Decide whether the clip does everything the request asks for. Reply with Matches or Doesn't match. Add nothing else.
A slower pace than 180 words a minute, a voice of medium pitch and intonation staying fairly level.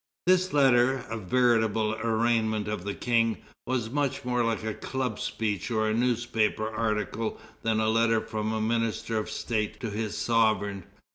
Doesn't match